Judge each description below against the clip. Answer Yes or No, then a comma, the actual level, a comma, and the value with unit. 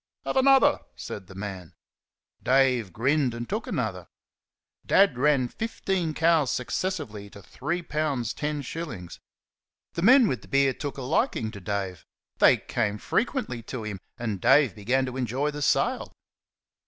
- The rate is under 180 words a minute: Yes, average, 150 wpm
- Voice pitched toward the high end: No, low, 130 Hz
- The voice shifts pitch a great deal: Yes, wide, 6.2 semitones